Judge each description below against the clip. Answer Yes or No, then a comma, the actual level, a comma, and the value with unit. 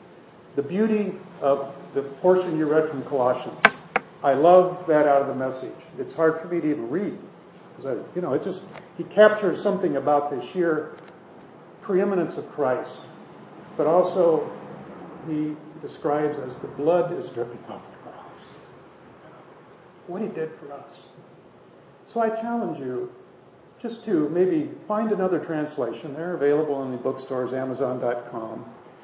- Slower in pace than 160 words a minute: Yes, average, 145 wpm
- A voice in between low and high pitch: Yes, medium, 160 Hz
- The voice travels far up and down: No, average, 4.7 semitones